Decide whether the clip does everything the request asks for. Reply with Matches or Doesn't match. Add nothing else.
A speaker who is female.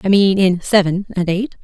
Matches